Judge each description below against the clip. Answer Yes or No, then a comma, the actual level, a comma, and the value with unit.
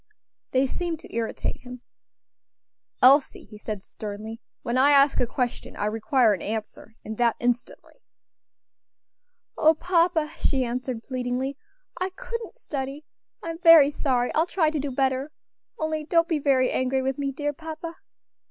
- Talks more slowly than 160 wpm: Yes, average, 150 wpm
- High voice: Yes, very high, 270 Hz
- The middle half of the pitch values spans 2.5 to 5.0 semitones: Yes, average, 4.2 semitones